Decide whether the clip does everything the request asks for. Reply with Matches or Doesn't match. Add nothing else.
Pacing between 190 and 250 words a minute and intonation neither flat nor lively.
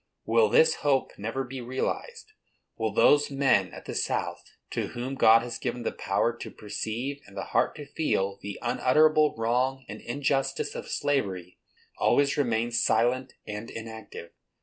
Doesn't match